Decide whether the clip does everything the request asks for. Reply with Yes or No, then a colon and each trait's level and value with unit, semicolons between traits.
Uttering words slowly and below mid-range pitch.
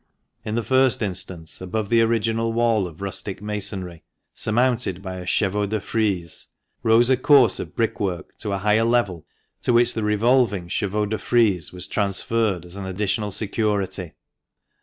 No: average, 160 wpm; low, 105 Hz